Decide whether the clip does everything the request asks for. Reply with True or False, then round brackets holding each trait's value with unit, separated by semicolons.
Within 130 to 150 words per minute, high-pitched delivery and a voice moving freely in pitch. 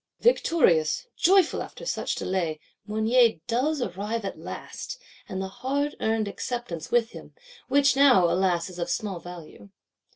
True (140 wpm; 220 Hz; 6.7 semitones)